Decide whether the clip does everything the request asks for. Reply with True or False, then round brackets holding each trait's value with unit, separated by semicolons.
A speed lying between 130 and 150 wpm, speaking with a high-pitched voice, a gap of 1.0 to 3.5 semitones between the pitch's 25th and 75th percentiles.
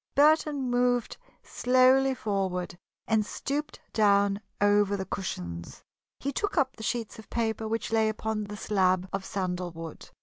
False (140 wpm; 215 Hz; 4.4 semitones)